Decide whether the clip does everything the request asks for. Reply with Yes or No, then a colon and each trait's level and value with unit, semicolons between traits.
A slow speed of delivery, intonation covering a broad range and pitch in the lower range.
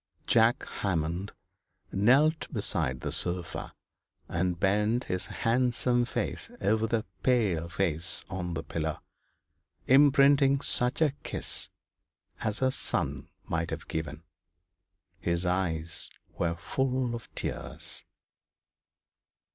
Yes: slow, 105 wpm; wide, 6.6 semitones; low, 100 Hz